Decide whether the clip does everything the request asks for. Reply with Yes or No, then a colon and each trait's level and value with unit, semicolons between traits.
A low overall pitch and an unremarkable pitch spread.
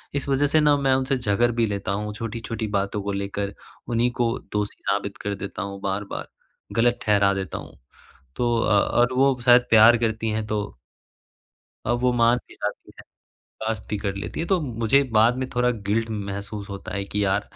Yes: low, 110 Hz; average, 3.2 semitones